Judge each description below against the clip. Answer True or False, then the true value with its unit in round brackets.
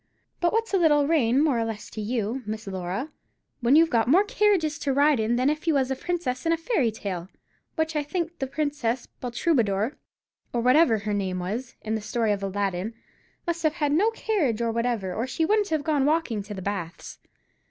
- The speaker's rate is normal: False (210 wpm)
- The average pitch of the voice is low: False (255 Hz)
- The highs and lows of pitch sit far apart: True (6.6 semitones)